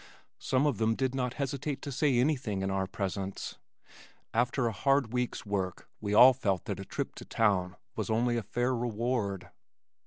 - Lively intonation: No, average, 4.6 semitones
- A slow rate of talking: No, average, 180 wpm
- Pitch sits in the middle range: No, low, 120 Hz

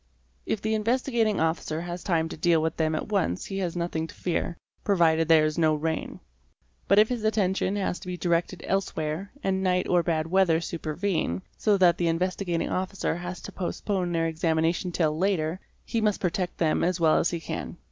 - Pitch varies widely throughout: No, average, 3.0 semitones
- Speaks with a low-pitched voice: No, medium, 175 Hz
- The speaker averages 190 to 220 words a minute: Yes, average, 200 wpm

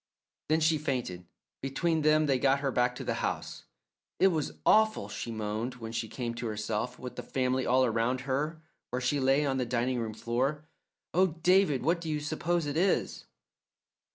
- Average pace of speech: Yes, average, 185 wpm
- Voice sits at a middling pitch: No, low, 130 Hz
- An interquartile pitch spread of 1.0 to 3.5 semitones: No, average, 4.2 semitones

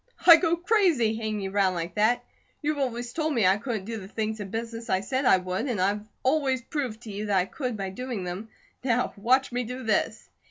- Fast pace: Yes, fast, 225 wpm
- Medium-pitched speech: No, high, 225 Hz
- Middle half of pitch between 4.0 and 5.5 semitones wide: Yes, average, 4.4 semitones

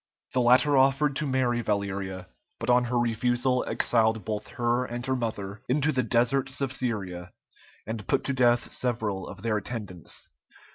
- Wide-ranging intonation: No, average, 3.1 semitones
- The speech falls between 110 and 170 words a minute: Yes, average, 160 wpm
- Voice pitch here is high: No, low, 120 Hz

